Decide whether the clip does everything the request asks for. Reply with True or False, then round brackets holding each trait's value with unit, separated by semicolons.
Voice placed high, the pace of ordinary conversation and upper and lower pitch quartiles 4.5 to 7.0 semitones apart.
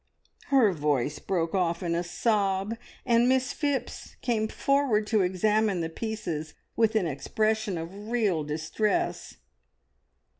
False (210 Hz; 125 wpm; 5.0 semitones)